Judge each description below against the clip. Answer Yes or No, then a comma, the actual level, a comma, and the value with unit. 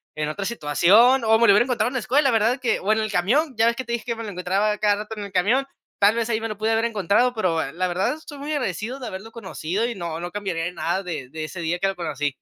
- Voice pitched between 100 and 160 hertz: No, high, 210 Hz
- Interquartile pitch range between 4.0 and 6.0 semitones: Yes, average, 4.6 semitones